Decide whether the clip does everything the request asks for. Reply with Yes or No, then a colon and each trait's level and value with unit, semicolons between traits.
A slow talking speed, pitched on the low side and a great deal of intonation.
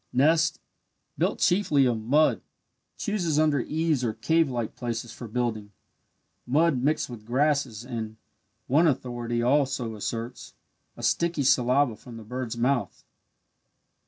No: slow, 125 wpm; low, 125 Hz; average, 4.2 semitones